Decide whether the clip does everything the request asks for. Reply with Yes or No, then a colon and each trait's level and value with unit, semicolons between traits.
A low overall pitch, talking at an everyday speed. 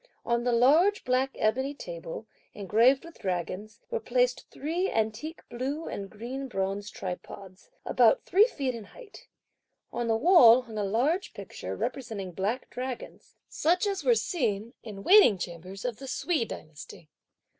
No: high, 240 Hz; average, 150 wpm